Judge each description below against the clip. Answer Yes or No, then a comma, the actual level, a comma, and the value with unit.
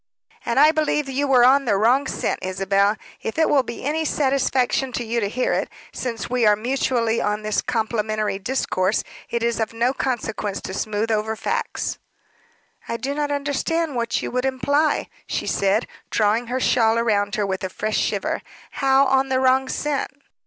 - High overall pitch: Yes, high, 235 Hz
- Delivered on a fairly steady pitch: No, average, 3.8 semitones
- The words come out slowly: No, average, 180 wpm